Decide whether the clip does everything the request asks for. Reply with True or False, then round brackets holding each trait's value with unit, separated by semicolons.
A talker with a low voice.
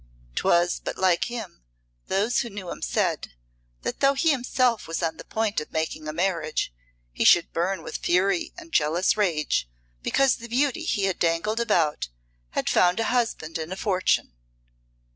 False (190 Hz)